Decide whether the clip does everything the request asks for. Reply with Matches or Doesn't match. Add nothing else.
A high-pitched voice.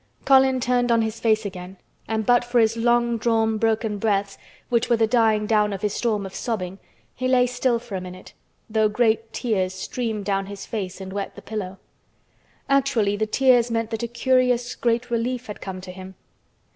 Matches